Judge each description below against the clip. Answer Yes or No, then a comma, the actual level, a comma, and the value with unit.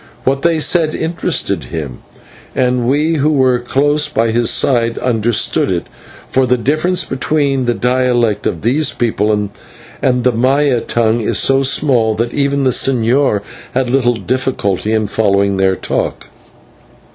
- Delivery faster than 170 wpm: No, average, 145 wpm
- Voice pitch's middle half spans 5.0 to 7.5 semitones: No, average, 3.5 semitones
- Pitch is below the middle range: Yes, low, 125 Hz